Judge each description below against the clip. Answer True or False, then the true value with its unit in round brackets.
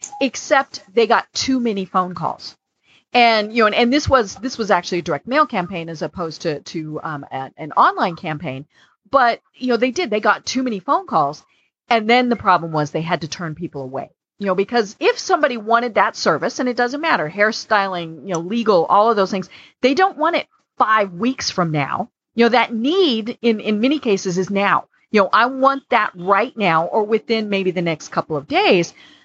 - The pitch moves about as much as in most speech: False (5.7 semitones)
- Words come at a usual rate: False (215 wpm)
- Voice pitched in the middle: False (210 Hz)